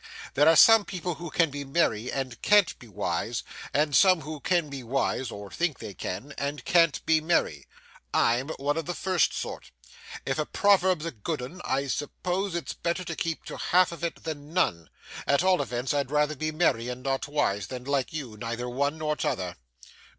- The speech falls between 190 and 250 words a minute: Yes, average, 200 wpm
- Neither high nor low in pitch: Yes, medium, 145 Hz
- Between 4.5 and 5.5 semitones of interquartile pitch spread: Yes, average, 4.8 semitones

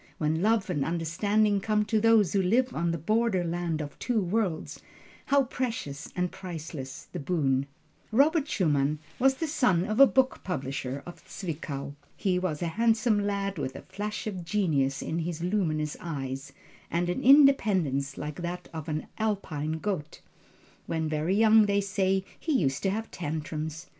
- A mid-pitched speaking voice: Yes, medium, 180 Hz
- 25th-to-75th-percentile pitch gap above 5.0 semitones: Yes, wide, 5.6 semitones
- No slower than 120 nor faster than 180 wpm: Yes, average, 165 wpm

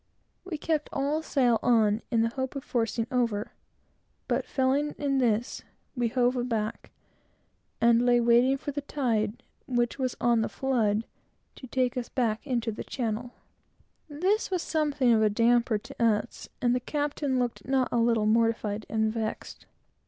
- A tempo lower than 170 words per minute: Yes, average, 160 wpm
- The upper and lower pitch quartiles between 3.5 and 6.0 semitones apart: No, average, 2.9 semitones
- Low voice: No, high, 240 Hz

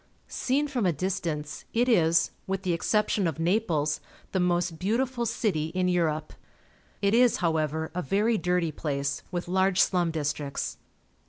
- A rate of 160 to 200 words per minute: No, average, 150 wpm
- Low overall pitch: No, medium, 180 Hz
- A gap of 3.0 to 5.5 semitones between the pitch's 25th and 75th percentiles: Yes, average, 4.0 semitones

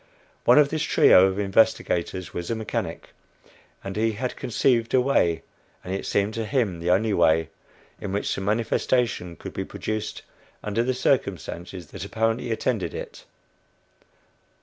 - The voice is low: Yes, low, 110 Hz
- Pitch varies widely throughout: No, average, 4.0 semitones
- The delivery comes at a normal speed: Yes, average, 150 wpm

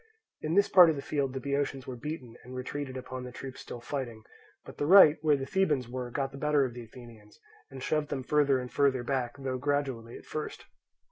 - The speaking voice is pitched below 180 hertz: Yes, low, 135 Hz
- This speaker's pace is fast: Yes, fast, 220 wpm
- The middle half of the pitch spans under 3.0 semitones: Yes, narrow, 2.5 semitones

